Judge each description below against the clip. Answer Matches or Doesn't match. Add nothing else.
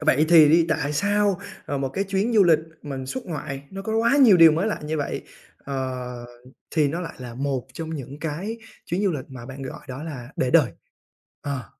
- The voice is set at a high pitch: Doesn't match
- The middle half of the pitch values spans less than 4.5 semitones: Doesn't match